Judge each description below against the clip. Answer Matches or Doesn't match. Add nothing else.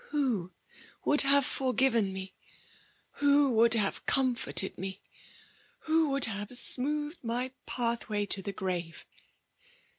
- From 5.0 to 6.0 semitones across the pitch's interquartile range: Matches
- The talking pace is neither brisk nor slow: Doesn't match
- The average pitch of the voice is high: Matches